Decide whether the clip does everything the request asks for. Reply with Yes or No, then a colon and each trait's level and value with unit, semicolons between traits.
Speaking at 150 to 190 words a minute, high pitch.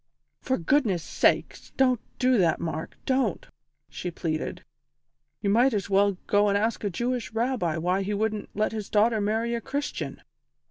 Yes: average, 165 wpm; high, 215 Hz